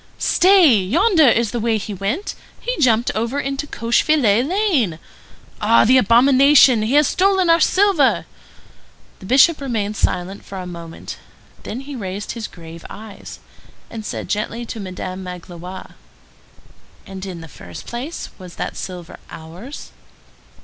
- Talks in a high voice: Yes, high, 230 Hz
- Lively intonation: Yes, wide, 6.9 semitones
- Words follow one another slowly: No, average, 145 wpm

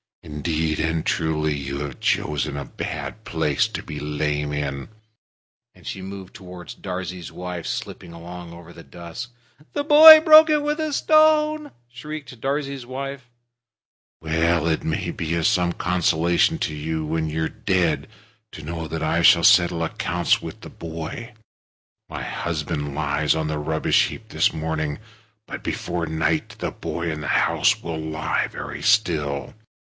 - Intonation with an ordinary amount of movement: Yes, average, 4.4 semitones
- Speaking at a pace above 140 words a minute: Yes, average, 150 wpm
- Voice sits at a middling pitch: No, very low, 85 Hz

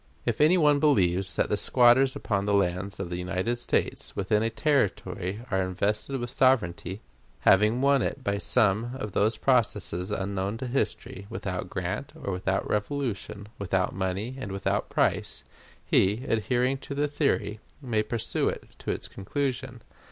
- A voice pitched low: Yes, low, 105 Hz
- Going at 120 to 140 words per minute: No, average, 160 wpm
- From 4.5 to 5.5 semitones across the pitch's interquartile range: Yes, average, 5.1 semitones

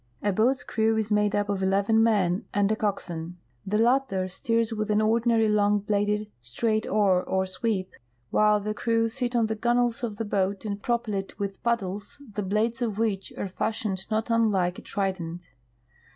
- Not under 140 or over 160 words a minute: No, average, 180 wpm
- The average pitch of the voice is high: Yes, high, 210 Hz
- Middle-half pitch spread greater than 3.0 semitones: No, narrow, 2.5 semitones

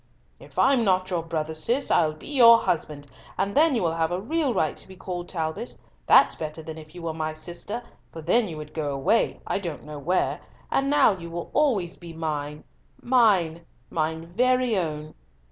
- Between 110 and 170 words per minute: No, average, 190 wpm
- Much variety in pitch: Yes, wide, 5.9 semitones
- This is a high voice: No, medium, 170 Hz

